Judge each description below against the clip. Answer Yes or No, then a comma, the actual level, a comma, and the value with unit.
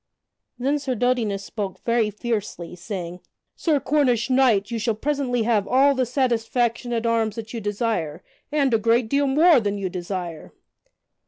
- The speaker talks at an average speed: Yes, average, 160 wpm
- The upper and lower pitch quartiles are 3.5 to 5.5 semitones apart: Yes, average, 3.8 semitones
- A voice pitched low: No, high, 230 Hz